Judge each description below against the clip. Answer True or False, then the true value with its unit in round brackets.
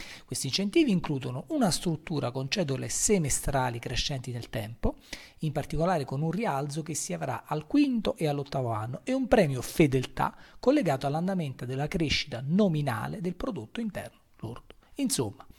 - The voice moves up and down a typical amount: False (6.2 semitones)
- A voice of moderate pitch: True (150 Hz)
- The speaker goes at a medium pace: True (145 wpm)